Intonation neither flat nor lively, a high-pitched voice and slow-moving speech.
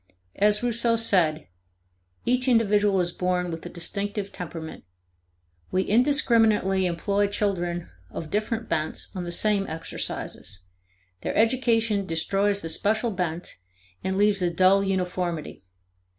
Yes: average, 3.5 semitones; high, 195 Hz; slow, 120 wpm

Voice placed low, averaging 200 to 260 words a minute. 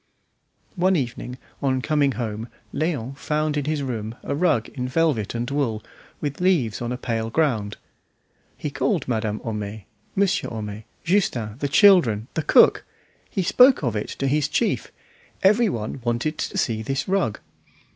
No: low, 130 Hz; average, 155 wpm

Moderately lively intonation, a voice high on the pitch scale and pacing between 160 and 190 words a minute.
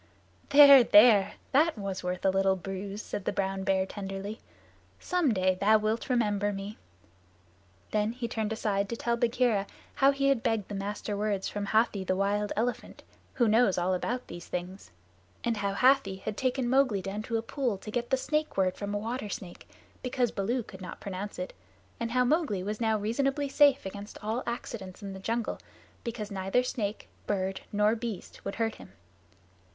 Yes: average, 3.6 semitones; high, 210 Hz; average, 185 wpm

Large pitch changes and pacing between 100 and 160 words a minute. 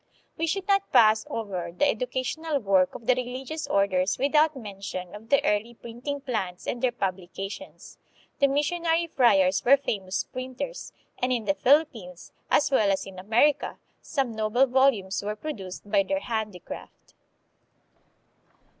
Yes: wide, 6.0 semitones; average, 150 wpm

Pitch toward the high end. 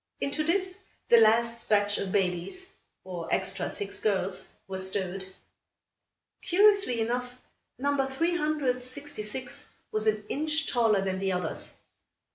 Yes: high, 230 Hz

